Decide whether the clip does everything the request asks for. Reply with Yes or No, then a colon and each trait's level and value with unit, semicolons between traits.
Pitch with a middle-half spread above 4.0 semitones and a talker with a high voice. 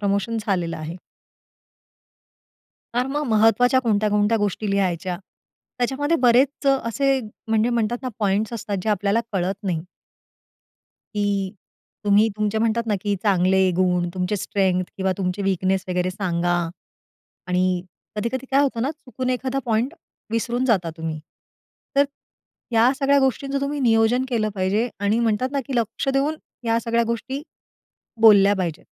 Yes: average, 4.5 semitones; high, 220 Hz